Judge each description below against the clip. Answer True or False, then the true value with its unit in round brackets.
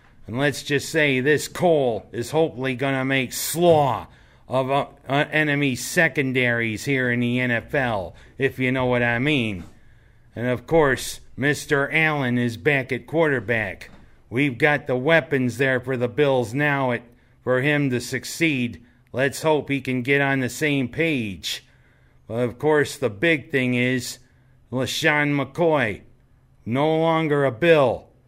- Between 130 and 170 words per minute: True (150 wpm)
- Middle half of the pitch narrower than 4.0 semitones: True (3.2 semitones)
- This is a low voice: True (130 Hz)